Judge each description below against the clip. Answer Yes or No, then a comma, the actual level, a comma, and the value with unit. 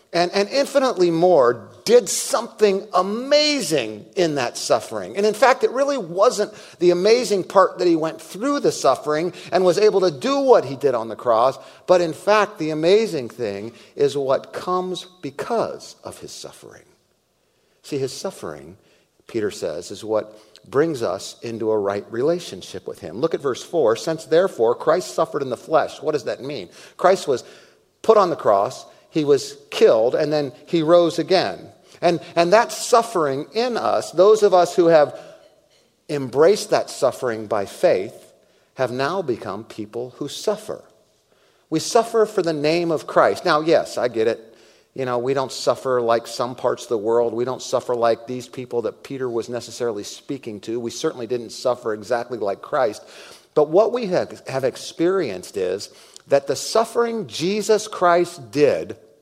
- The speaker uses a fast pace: No, average, 170 wpm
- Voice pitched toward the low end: No, medium, 180 Hz